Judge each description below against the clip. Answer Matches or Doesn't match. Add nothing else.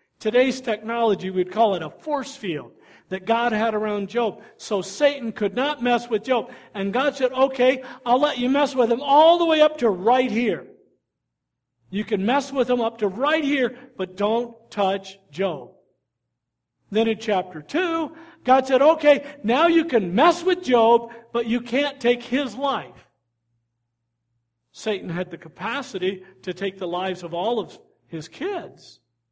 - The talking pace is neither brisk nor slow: Matches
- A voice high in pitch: Matches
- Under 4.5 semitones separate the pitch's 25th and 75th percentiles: Doesn't match